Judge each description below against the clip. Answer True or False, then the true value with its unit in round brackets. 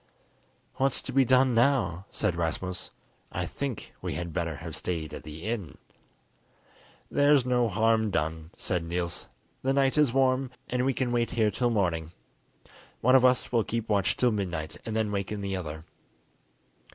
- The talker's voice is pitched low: True (105 Hz)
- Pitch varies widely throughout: True (6.7 semitones)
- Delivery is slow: False (165 wpm)